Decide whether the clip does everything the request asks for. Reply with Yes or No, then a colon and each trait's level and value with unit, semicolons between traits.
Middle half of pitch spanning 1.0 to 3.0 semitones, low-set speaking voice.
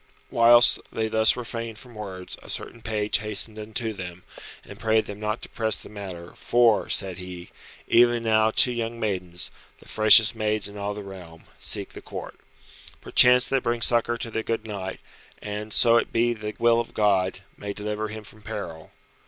Yes: narrow, 2.4 semitones; low, 110 Hz